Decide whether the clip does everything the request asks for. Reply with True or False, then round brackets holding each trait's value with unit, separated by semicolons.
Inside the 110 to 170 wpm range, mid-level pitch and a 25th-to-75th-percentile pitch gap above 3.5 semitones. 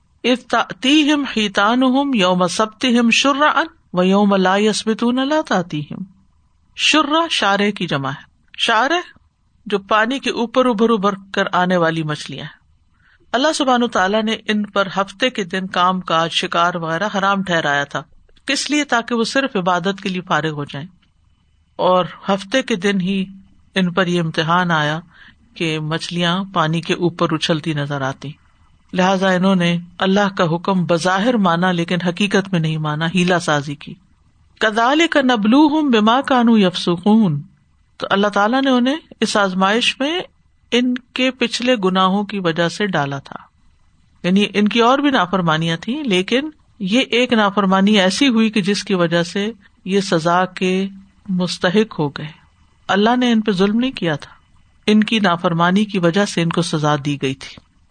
False (160 wpm; 195 Hz; 5.1 semitones)